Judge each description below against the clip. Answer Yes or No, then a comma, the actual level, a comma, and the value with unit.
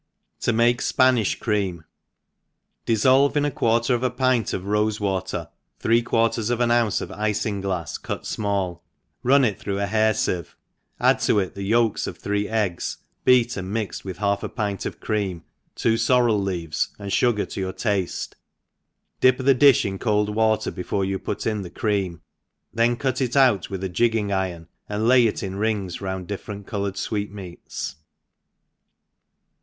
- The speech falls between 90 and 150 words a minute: No, average, 170 wpm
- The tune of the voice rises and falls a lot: No, average, 3.3 semitones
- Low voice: Yes, low, 105 Hz